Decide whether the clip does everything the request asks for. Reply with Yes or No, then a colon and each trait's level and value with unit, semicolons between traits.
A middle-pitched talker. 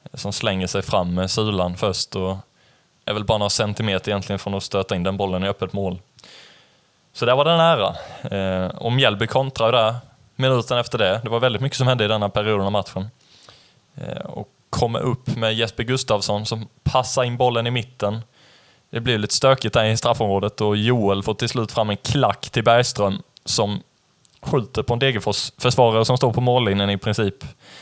No: low, 110 Hz